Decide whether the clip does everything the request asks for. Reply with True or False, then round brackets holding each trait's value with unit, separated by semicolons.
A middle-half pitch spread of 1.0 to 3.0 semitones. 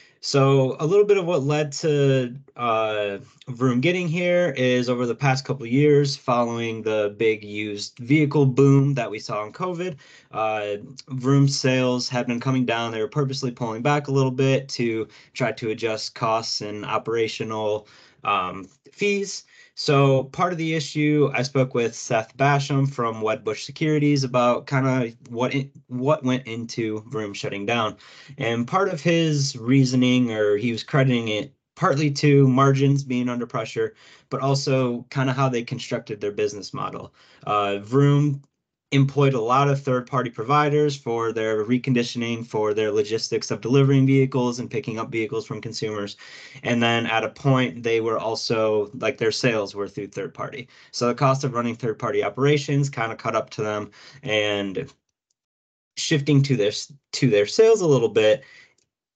False (3.8 semitones)